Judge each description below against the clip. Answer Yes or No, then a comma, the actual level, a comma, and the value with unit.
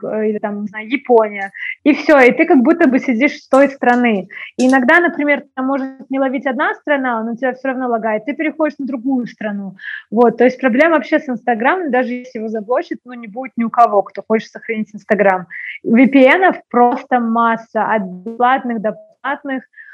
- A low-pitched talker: No, very high, 250 Hz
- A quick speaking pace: Yes, fast, 185 wpm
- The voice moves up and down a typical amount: Yes, average, 3.7 semitones